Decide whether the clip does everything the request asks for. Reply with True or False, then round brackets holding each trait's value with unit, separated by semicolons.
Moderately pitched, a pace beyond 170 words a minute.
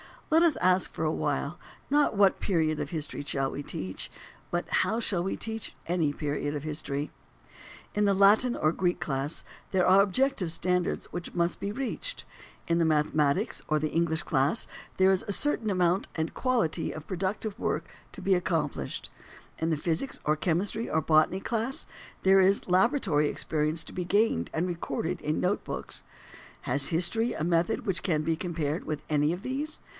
True (175 Hz; 180 wpm)